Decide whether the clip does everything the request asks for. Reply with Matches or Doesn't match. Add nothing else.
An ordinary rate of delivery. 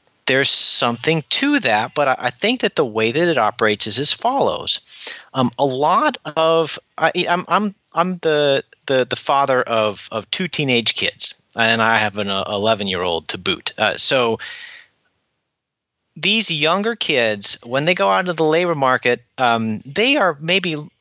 Matches